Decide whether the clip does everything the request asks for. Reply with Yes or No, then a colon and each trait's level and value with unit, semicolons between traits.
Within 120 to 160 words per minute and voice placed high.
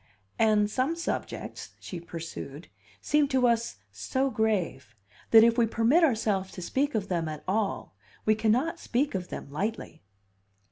Yes: average, 150 wpm; high, 220 Hz